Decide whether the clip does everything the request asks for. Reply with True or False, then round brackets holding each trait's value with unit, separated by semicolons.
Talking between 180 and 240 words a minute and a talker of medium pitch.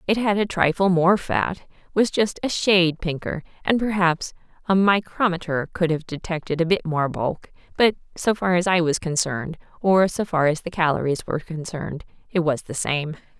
True (185 wpm; 175 Hz)